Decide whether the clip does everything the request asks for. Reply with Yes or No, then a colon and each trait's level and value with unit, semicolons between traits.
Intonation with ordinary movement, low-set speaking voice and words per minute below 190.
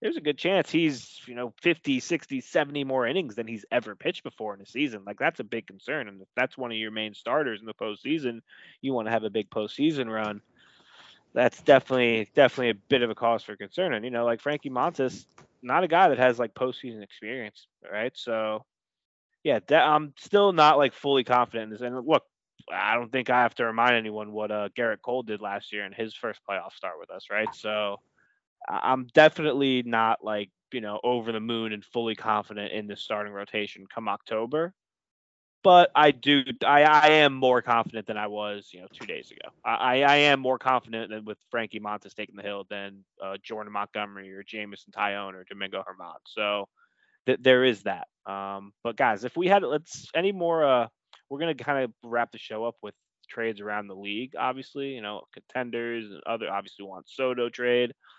No: average, 3.8 semitones; low, 115 Hz; fast, 205 wpm